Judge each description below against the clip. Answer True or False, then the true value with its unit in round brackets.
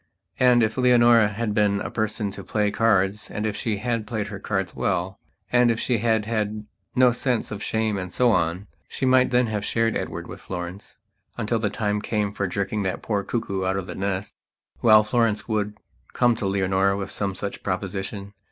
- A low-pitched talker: True (105 Hz)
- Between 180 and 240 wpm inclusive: True (200 wpm)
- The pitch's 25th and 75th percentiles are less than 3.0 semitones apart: True (2.6 semitones)